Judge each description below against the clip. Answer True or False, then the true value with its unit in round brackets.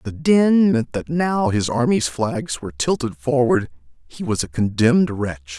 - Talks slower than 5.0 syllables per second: True (4.4 syllables/s)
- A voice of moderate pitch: False (125 Hz)